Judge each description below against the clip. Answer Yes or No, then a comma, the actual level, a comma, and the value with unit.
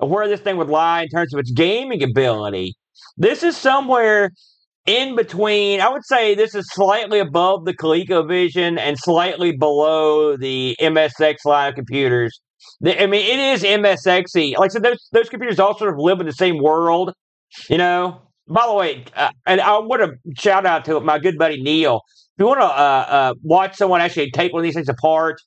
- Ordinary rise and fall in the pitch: Yes, average, 4.7 semitones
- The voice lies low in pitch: No, medium, 175 Hz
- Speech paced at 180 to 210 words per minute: Yes, average, 200 wpm